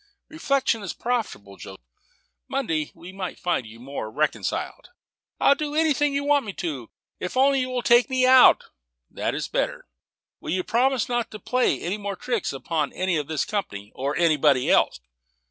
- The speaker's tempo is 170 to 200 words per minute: Yes, average, 175 wpm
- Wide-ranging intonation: Yes, wide, 8.9 semitones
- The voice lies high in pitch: Yes, high, 200 Hz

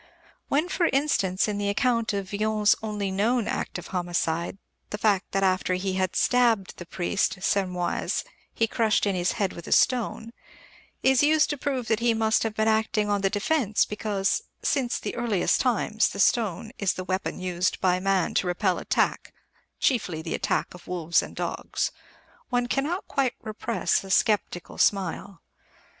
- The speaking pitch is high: Yes, high, 205 Hz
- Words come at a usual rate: Yes, average, 170 wpm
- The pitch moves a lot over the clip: No, average, 3.8 semitones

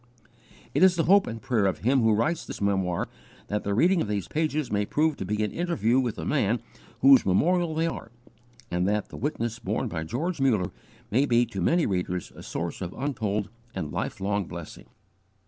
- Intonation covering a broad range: Yes, wide, 7.3 semitones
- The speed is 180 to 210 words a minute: Yes, average, 200 wpm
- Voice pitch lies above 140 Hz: No, low, 115 Hz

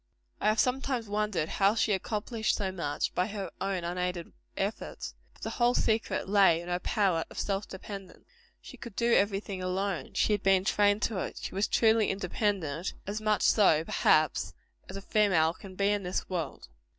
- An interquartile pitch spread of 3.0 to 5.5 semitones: No, narrow, 2.6 semitones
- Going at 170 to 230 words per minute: Yes, average, 185 wpm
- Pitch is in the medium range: No, high, 195 Hz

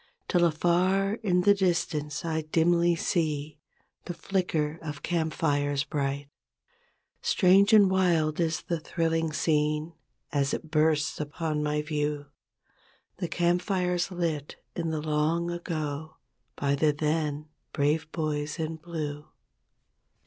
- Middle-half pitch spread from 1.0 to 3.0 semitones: Yes, narrow, 2.4 semitones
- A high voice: No, medium, 160 Hz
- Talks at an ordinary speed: No, slow, 125 wpm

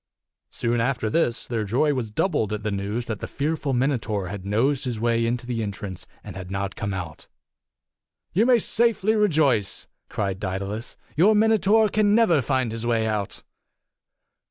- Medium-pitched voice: No, low, 120 Hz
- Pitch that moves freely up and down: Yes, wide, 6.8 semitones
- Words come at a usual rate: Yes, average, 165 wpm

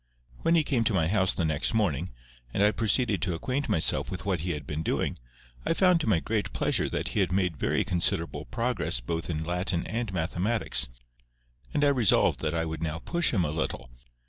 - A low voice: Yes, very low, 90 Hz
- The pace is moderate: No, fast, 210 wpm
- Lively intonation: Yes, wide, 5.8 semitones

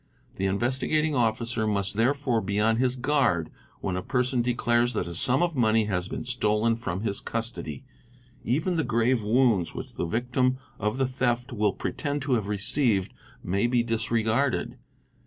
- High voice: No, low, 120 Hz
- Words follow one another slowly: No, average, 165 wpm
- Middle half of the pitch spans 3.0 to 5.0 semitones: Yes, average, 3.3 semitones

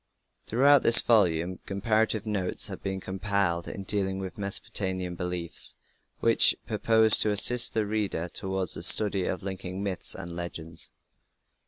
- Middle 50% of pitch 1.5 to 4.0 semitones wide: Yes, average, 2.8 semitones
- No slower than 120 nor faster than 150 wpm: Yes, average, 140 wpm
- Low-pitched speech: Yes, very low, 95 Hz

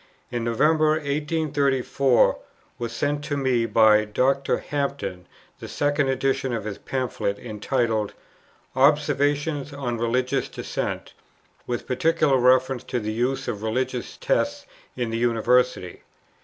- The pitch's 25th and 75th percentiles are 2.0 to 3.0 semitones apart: No, average, 3.5 semitones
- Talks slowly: Yes, slow, 120 wpm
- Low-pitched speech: Yes, low, 130 Hz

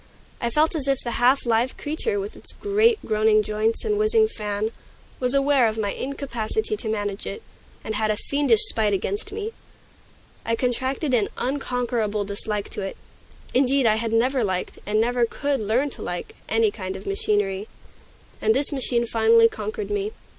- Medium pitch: No, high, 240 Hz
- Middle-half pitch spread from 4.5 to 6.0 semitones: Yes, average, 5.1 semitones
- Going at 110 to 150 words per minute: No, average, 175 wpm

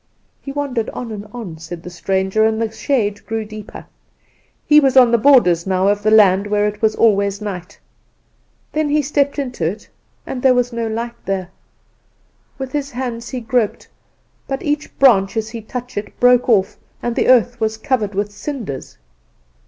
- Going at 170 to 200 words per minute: Yes, average, 180 wpm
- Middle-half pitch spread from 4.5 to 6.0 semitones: No, average, 3.7 semitones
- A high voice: Yes, high, 220 Hz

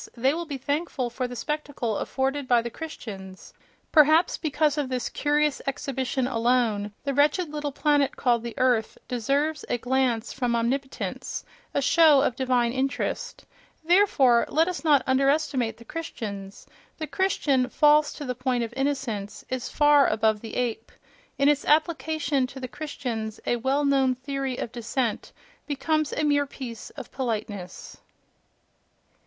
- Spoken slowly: No, average, 150 wpm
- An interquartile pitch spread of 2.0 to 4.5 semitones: Yes, average, 3.5 semitones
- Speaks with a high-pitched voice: Yes, very high, 265 Hz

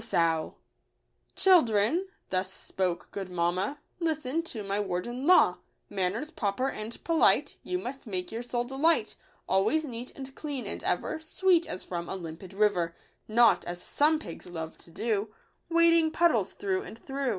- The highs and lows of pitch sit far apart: Yes, wide, 8.9 semitones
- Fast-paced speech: No, average, 165 wpm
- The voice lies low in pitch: No, high, 235 Hz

